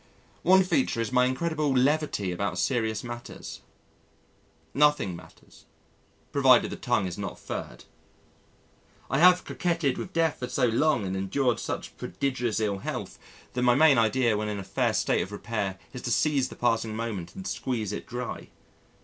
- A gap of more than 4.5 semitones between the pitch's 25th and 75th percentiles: Yes, wide, 5.5 semitones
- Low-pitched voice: Yes, low, 120 Hz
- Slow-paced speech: No, average, 165 wpm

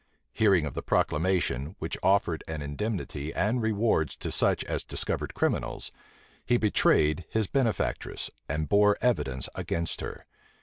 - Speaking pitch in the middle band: No, very low, 90 Hz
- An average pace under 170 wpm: Yes, slow, 135 wpm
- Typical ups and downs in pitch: No, wide, 5.9 semitones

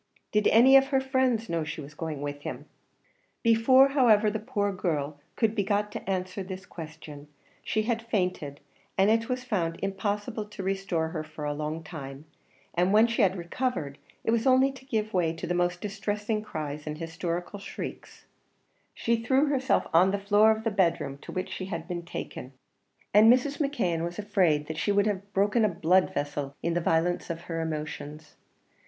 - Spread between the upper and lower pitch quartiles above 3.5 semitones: Yes, average, 5.2 semitones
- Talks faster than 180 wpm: Yes, average, 190 wpm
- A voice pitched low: No, high, 190 Hz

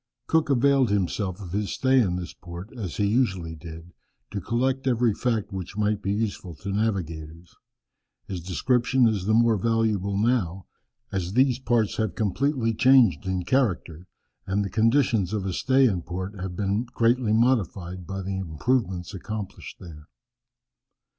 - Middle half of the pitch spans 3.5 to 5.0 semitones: Yes, average, 4.4 semitones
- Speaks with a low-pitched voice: Yes, low, 100 Hz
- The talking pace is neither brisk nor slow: Yes, average, 155 wpm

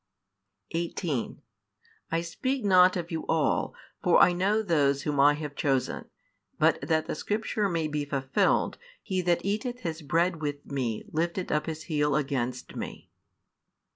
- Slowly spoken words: No, average, 150 wpm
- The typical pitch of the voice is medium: Yes, medium, 160 Hz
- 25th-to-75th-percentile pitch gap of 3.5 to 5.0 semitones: Yes, average, 3.8 semitones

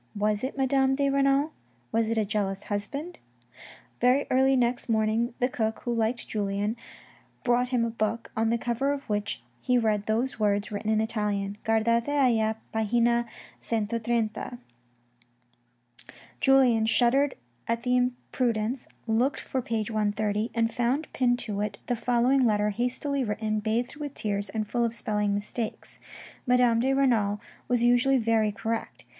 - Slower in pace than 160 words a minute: Yes, average, 150 wpm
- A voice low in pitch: No, high, 230 Hz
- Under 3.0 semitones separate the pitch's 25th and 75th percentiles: Yes, narrow, 2.6 semitones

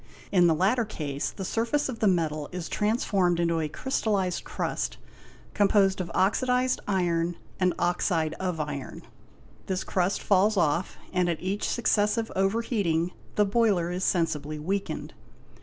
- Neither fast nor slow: Yes, average, 145 wpm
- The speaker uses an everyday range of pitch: Yes, average, 3.6 semitones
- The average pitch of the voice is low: No, medium, 185 Hz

